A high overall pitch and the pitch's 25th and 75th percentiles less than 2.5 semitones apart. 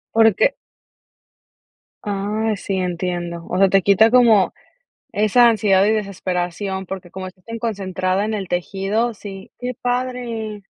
No: high, 200 Hz; average, 2.9 semitones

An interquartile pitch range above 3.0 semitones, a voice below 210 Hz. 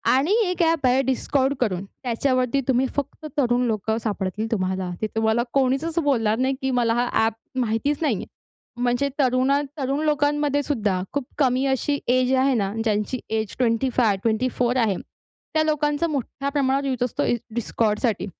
No: average, 3.8 semitones; very high, 255 Hz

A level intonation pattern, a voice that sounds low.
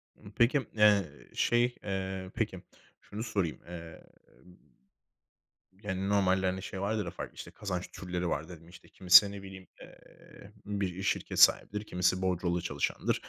Yes: narrow, 2.3 semitones; very low, 95 Hz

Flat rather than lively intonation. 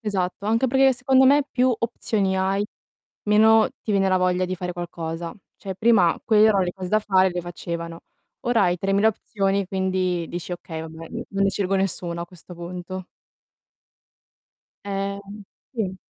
No: average, 3.0 semitones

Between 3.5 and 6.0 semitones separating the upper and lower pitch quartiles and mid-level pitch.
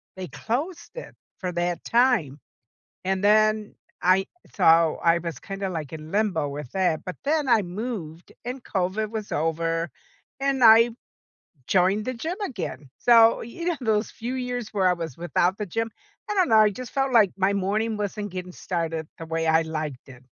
No: wide, 5.4 semitones; high, 195 Hz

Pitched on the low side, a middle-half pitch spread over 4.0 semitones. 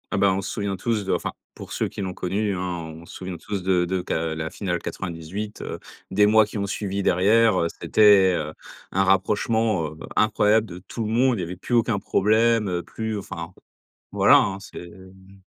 No: very low, 95 Hz; average, 2.9 semitones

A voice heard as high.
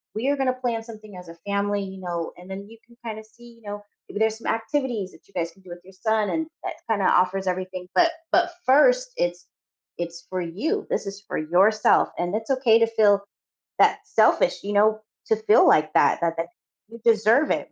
Yes: high, 210 Hz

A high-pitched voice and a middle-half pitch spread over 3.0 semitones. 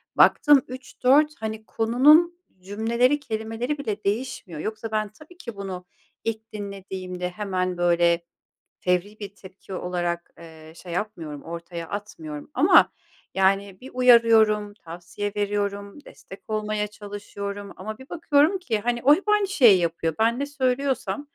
Yes: high, 210 Hz; average, 5.2 semitones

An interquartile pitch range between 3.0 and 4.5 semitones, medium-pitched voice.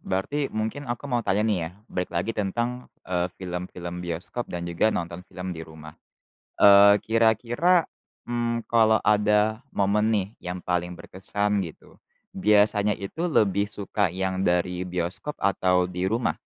No: average, 3.6 semitones; low, 100 Hz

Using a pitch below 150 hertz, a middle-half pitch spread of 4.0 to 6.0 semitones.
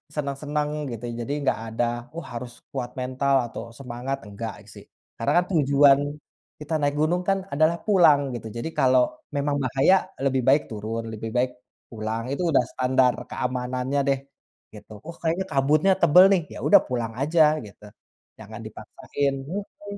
No: low, 135 Hz; average, 3.4 semitones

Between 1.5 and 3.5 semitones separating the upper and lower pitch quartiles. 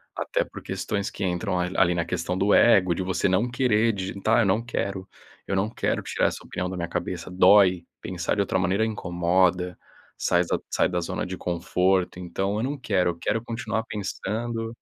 Yes: average, 3.1 semitones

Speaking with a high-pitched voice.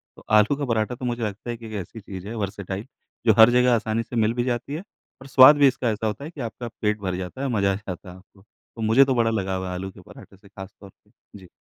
No: low, 110 Hz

